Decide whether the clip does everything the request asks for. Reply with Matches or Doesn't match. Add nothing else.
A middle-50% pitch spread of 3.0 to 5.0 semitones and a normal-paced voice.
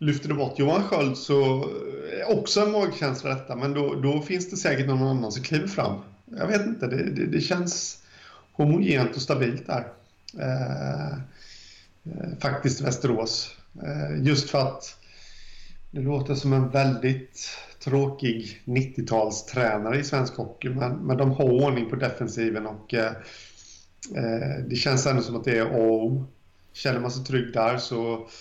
Matches